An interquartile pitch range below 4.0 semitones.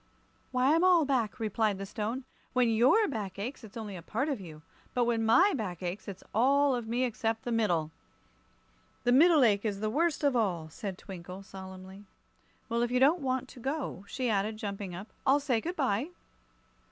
No: average, 4.8 semitones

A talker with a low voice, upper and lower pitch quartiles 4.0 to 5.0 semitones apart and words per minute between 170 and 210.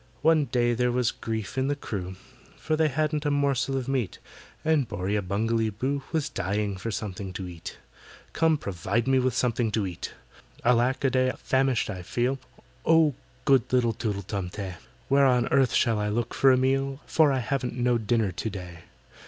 Yes: low, 120 Hz; average, 4.5 semitones; average, 185 wpm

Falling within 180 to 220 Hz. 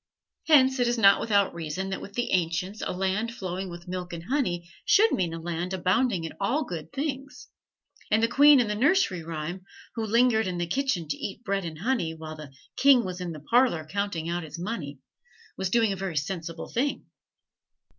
Yes: high, 190 Hz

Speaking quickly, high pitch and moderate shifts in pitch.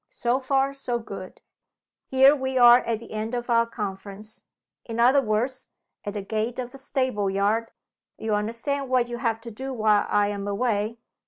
No: average, 180 wpm; high, 230 Hz; average, 3.2 semitones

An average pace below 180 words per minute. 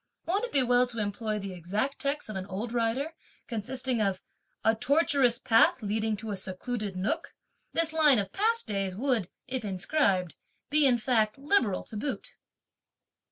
Yes: average, 165 wpm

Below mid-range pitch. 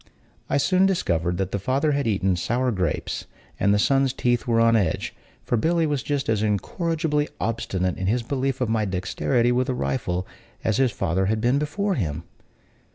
Yes: low, 120 Hz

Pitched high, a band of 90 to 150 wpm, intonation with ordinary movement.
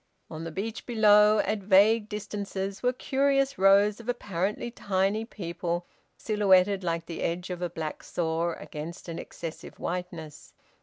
Yes: high, 195 Hz; average, 145 wpm; average, 3.8 semitones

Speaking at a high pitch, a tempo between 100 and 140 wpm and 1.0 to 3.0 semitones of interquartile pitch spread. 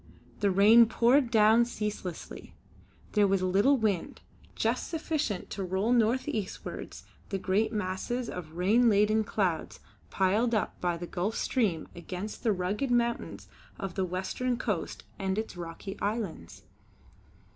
No: high, 205 Hz; slow, 135 wpm; average, 3.9 semitones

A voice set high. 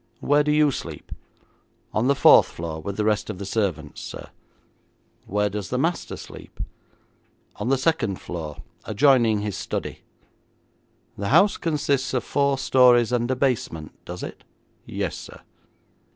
No: low, 120 Hz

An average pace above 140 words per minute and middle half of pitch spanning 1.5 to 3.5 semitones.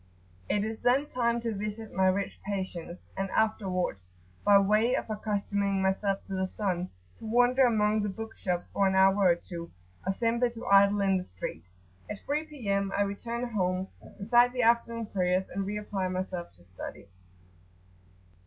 Yes: average, 170 wpm; average, 3.0 semitones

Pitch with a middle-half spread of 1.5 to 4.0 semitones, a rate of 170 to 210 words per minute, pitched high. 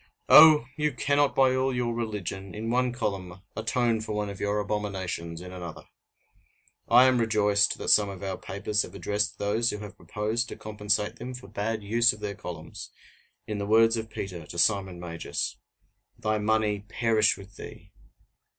No: narrow, 2.6 semitones; average, 175 wpm; low, 105 Hz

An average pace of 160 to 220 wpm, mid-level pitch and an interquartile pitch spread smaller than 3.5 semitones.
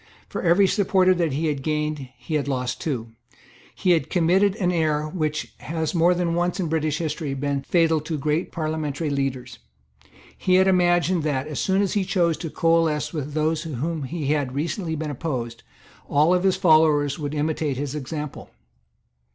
Yes: average, 175 wpm; medium, 155 Hz; average, 2.9 semitones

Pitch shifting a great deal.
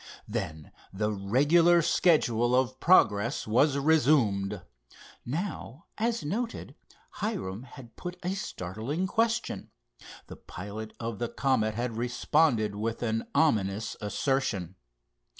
Yes: wide, 6.9 semitones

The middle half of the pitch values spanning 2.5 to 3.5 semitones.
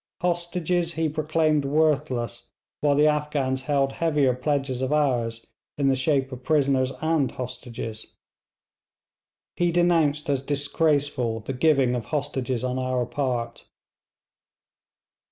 Yes: average, 3.1 semitones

